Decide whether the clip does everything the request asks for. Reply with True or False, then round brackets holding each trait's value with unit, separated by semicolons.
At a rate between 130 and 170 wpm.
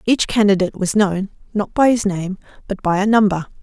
False (200 wpm)